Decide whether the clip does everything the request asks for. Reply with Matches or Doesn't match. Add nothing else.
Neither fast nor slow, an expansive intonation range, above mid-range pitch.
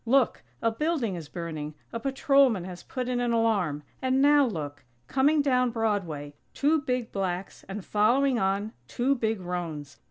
Matches